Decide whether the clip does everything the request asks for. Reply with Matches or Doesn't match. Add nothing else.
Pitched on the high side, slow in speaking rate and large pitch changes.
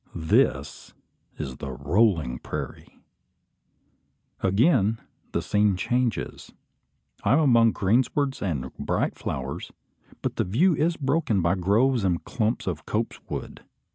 Doesn't match